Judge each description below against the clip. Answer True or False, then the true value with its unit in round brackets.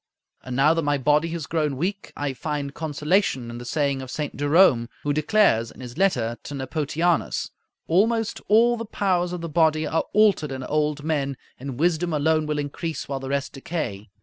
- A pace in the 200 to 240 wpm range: False (190 wpm)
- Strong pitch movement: False (3.6 semitones)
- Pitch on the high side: False (150 Hz)